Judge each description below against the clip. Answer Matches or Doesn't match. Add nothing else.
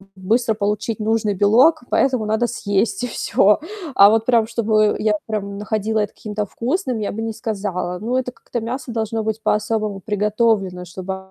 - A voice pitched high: Matches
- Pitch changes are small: Matches